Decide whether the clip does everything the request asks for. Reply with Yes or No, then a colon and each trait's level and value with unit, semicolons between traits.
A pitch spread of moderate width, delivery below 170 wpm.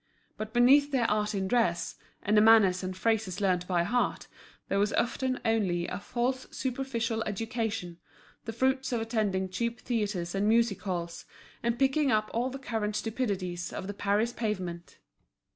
Yes: average, 4.0 semitones; average, 160 wpm